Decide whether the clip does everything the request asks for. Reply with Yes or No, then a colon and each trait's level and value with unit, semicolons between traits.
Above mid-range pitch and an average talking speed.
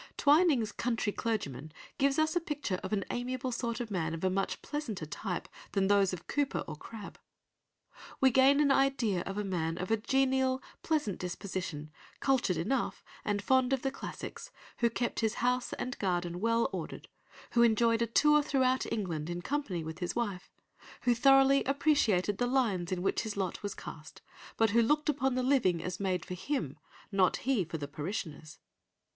Yes: high, 225 Hz; average, 185 wpm